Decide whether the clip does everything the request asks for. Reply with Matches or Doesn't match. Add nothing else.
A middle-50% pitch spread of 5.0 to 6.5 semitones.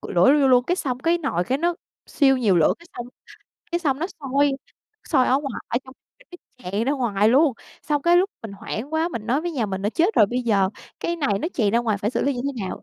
Matches